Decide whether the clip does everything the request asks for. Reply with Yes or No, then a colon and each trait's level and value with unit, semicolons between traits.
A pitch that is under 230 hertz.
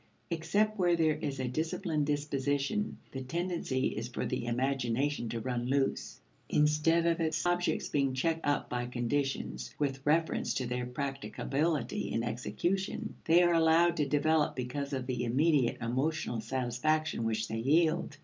Yes: medium, 140 Hz